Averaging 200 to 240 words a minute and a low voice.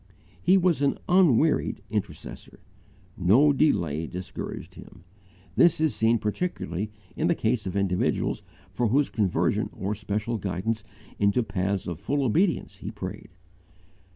No: slow, 135 wpm; low, 110 Hz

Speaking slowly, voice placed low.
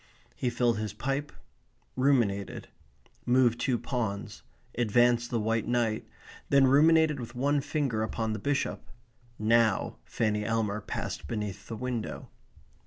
Yes: slow, 125 wpm; low, 120 Hz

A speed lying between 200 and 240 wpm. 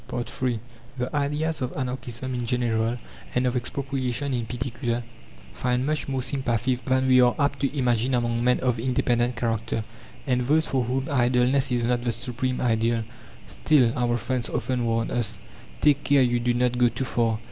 No: average, 175 wpm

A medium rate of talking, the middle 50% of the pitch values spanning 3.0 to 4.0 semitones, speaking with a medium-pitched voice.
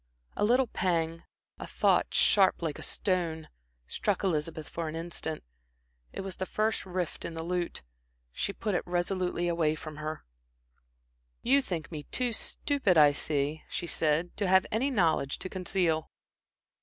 Yes: average, 155 wpm; average, 3.3 semitones; medium, 175 Hz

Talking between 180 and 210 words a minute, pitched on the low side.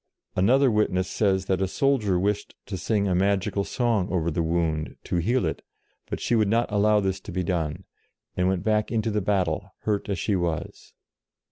Yes: average, 195 wpm; very low, 95 Hz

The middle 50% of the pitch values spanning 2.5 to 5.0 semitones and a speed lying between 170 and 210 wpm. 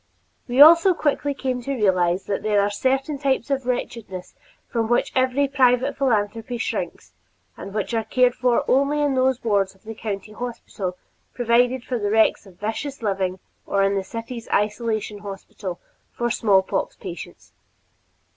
No: average, 4.2 semitones; average, 155 wpm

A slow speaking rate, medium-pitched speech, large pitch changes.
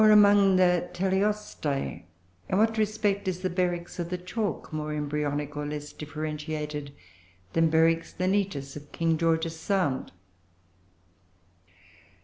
No: slow, 125 wpm; medium, 165 Hz; average, 4.3 semitones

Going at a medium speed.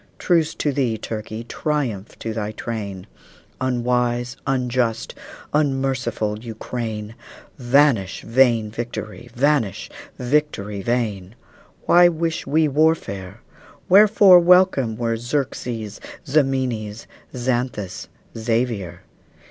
No: slow, 90 wpm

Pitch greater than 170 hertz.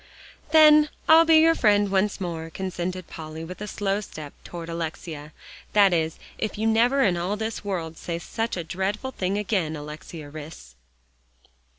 Yes: medium, 185 Hz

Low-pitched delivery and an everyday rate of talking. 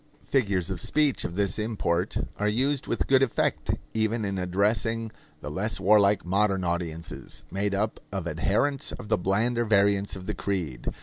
Yes: low, 100 Hz; average, 165 wpm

